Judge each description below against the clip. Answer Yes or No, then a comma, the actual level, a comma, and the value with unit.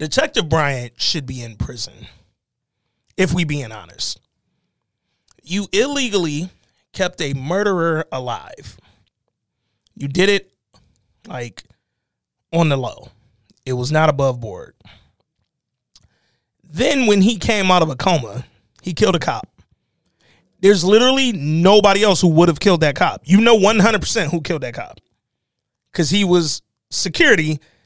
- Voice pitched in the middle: Yes, medium, 160 Hz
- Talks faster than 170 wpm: No, average, 140 wpm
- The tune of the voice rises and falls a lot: Yes, wide, 7.8 semitones